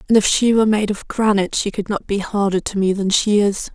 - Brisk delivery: Yes, fast, 275 wpm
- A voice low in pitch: No, high, 205 Hz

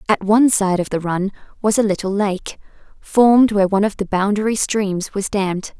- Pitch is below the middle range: No, high, 205 Hz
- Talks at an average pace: Yes, average, 195 wpm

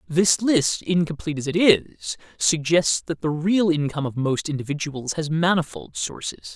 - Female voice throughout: No, male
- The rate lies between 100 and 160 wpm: Yes, average, 155 wpm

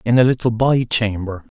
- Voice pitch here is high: No, low, 115 Hz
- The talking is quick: No, average, 190 wpm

